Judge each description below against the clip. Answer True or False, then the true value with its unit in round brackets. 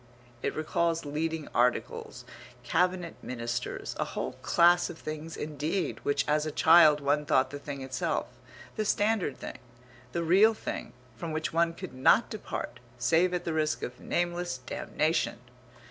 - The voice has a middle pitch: True (155 Hz)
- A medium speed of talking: True (150 wpm)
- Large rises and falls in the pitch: False (3.4 semitones)